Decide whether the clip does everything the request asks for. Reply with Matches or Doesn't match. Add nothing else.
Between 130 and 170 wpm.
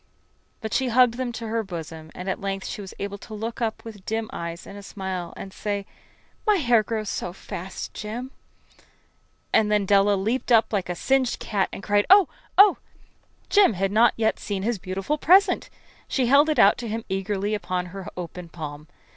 Doesn't match